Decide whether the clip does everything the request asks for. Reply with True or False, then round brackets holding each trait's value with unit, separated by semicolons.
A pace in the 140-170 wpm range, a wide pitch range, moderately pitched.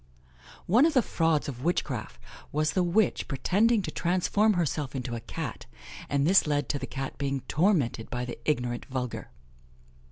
True (165 wpm; 5.8 semitones; 150 Hz)